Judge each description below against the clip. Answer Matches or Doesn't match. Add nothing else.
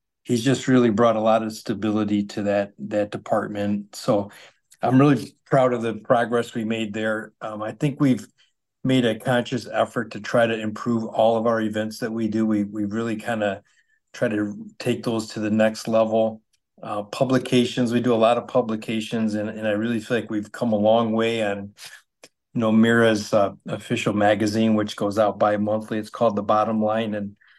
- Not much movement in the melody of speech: Matches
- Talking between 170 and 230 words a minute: Matches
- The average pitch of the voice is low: Matches